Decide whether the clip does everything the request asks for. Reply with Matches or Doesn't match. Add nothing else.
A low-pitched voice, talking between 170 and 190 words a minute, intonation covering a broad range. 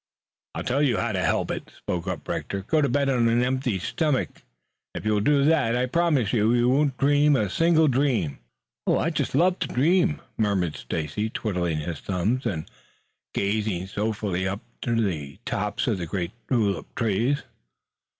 Matches